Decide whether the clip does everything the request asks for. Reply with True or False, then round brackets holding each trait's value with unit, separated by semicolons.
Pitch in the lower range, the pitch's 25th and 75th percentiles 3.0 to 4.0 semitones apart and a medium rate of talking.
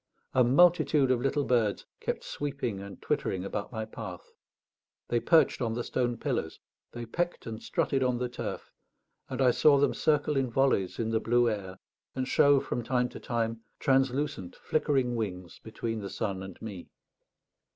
True (120 Hz; 3.5 semitones; 170 wpm)